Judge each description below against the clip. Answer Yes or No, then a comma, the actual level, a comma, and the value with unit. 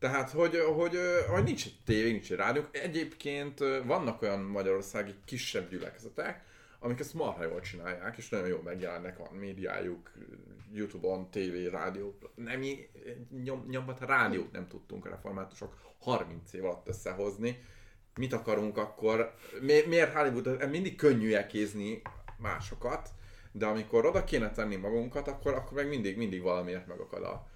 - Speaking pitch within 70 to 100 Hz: No, low, 115 Hz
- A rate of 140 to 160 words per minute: Yes, average, 145 wpm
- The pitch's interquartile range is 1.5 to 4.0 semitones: No, wide, 5.5 semitones